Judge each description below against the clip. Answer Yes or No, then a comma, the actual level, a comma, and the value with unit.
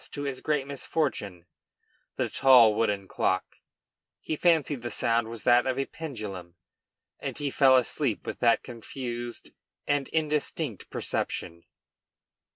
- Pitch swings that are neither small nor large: Yes, average, 4.2 semitones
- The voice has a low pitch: Yes, low, 125 Hz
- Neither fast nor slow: No, slow, 130 wpm